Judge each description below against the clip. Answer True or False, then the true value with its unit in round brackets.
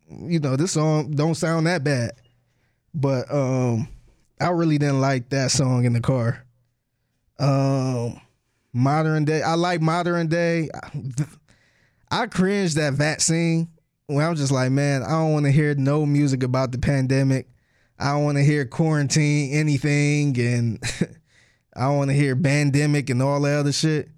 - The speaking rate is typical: True (160 wpm)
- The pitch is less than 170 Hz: True (140 Hz)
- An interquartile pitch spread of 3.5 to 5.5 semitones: False (3.1 semitones)